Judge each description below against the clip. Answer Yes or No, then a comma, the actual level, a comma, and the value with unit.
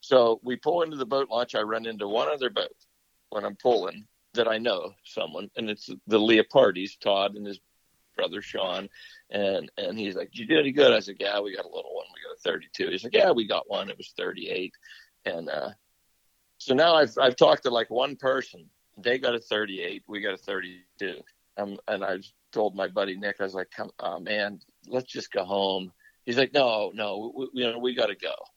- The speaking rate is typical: No, fast, 220 wpm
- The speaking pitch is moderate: No, low, 120 Hz